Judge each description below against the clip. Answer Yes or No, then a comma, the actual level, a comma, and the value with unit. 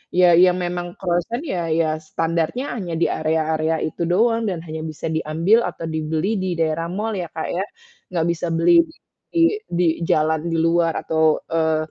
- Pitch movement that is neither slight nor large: No, narrow, 2.3 semitones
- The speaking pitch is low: No, medium, 165 Hz